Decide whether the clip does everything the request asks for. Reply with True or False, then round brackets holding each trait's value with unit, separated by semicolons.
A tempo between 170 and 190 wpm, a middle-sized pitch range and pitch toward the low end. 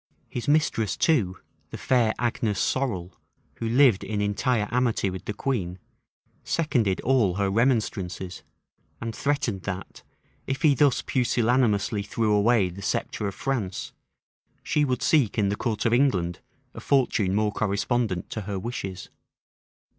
False (140 wpm; 4.3 semitones; 110 Hz)